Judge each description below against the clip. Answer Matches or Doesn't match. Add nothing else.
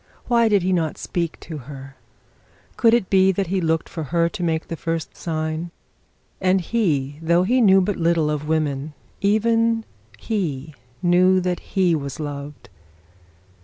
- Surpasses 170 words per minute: Doesn't match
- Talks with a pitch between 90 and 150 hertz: Doesn't match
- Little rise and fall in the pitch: Doesn't match